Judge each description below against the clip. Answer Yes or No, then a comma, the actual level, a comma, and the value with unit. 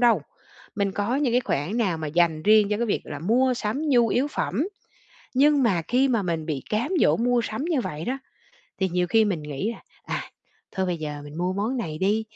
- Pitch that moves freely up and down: Yes, wide, 6.1 semitones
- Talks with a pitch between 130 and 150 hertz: No, high, 210 Hz